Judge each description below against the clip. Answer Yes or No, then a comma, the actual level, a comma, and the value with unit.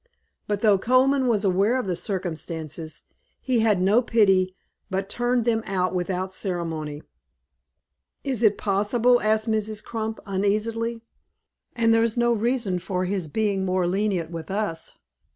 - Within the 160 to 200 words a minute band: No, average, 140 wpm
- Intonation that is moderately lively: Yes, average, 3.7 semitones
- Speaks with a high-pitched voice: Yes, high, 205 Hz